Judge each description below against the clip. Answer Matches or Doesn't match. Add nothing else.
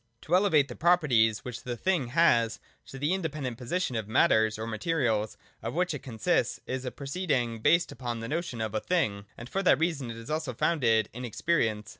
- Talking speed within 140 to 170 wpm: Doesn't match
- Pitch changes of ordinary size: Doesn't match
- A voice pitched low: Matches